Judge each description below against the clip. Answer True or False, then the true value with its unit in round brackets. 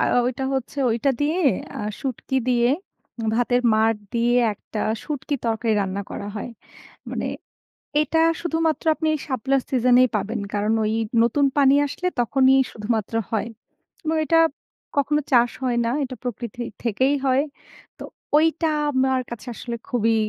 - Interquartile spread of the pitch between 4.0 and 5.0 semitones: False (3.5 semitones)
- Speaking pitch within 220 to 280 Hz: True (250 Hz)